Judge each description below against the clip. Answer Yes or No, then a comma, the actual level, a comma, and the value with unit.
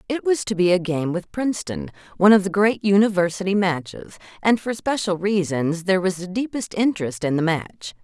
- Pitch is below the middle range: No, medium, 185 Hz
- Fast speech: No, average, 195 wpm